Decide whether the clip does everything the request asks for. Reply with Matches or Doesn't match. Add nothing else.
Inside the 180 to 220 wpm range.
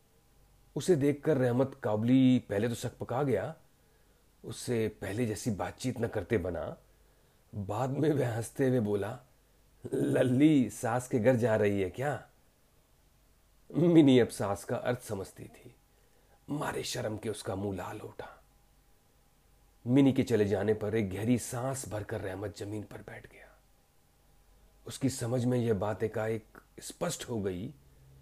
Doesn't match